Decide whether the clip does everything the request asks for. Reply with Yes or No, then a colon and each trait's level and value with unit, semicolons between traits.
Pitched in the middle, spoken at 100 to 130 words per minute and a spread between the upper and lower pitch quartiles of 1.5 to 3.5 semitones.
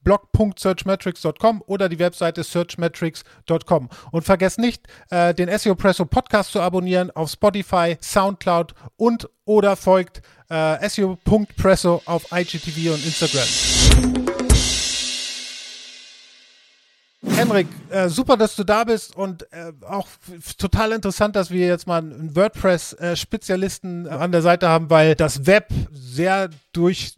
Yes: medium, 180 Hz; slow, 125 wpm; average, 2.9 semitones